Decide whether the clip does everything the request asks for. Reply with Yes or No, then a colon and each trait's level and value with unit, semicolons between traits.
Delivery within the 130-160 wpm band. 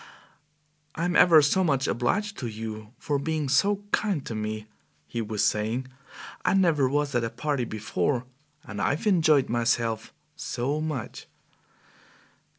Yes: average, 140 wpm